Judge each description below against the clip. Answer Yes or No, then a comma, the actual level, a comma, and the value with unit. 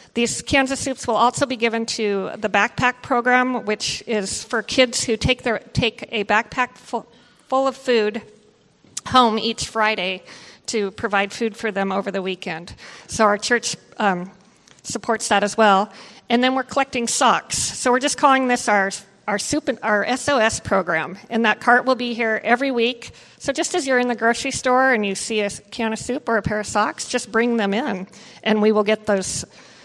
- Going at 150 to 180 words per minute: No, average, 200 wpm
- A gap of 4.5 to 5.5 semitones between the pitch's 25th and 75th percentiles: No, average, 3.1 semitones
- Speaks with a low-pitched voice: No, high, 225 Hz